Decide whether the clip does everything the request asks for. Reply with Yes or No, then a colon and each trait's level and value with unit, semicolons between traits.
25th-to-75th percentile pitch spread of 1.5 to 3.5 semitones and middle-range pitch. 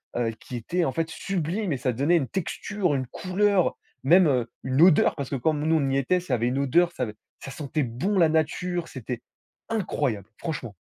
No: wide, 5.5 semitones; medium, 150 Hz